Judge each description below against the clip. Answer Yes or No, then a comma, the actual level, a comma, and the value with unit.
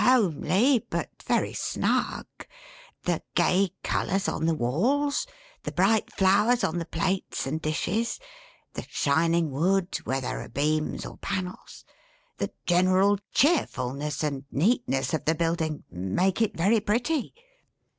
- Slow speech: Yes, slow, 130 wpm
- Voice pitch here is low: No, medium, 180 Hz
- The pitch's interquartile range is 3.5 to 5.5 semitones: Yes, average, 5.2 semitones